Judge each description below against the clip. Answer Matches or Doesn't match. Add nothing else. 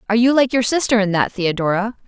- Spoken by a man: Doesn't match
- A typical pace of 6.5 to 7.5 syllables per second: Matches